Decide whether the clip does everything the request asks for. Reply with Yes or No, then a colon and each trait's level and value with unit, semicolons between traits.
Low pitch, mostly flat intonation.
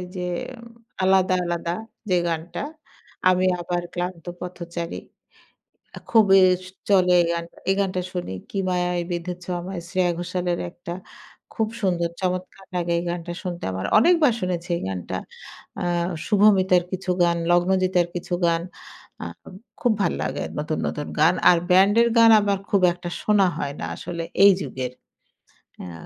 No: medium, 180 Hz; narrow, 1.7 semitones